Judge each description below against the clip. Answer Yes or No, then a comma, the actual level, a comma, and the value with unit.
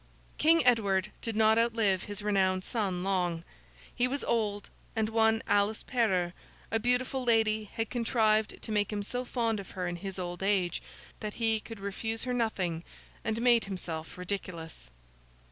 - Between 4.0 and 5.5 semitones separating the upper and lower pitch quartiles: No, average, 3.1 semitones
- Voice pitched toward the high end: Yes, high, 215 Hz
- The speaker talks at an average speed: Yes, average, 160 wpm